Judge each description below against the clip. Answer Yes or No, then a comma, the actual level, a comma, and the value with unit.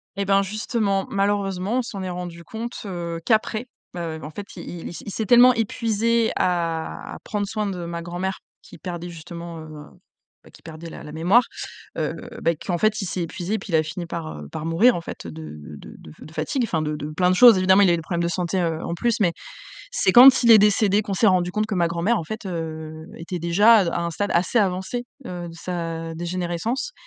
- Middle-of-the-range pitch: Yes, medium, 180 Hz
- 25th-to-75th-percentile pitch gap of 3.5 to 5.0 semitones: Yes, average, 3.9 semitones